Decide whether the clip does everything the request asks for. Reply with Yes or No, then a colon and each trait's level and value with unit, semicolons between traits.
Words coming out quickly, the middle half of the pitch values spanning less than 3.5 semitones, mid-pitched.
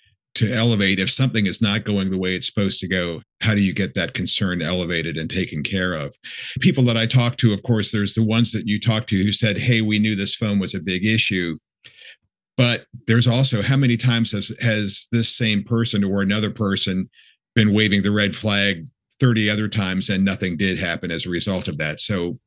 No: fast, 215 wpm; average, 2.8 semitones; low, 105 Hz